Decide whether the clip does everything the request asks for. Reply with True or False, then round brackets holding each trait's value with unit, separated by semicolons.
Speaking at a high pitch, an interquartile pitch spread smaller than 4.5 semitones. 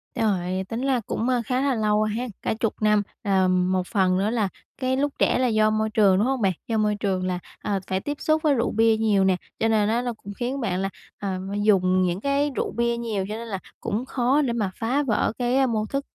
True (220 Hz; 4.0 semitones)